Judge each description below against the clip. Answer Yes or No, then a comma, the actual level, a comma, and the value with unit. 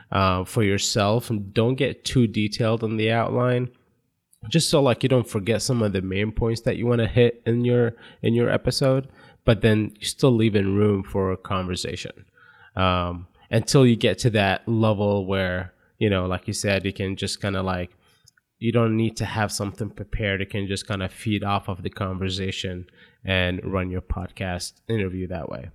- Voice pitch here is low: Yes, low, 105 Hz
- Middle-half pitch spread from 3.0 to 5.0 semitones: Yes, average, 3.4 semitones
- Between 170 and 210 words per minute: Yes, average, 200 wpm